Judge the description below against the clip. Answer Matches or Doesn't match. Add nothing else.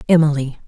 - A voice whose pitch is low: Doesn't match